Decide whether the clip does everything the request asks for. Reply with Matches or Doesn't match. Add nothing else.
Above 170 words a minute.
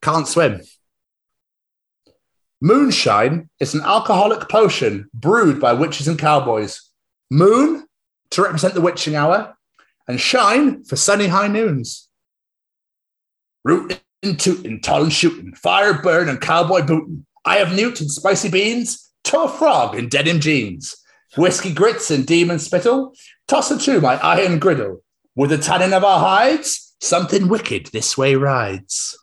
Doesn't match